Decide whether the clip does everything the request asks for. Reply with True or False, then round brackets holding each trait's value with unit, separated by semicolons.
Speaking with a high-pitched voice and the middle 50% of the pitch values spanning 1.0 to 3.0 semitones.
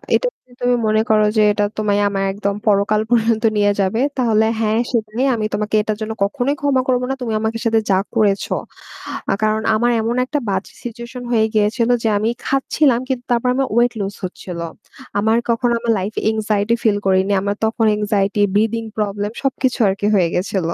True (220 Hz; 2.6 semitones)